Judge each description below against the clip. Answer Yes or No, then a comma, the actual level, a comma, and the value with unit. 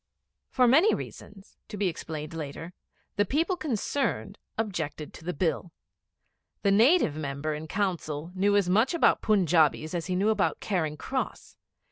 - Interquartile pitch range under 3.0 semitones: No, average, 5.2 semitones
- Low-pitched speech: No, medium, 185 Hz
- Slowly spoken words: No, average, 150 wpm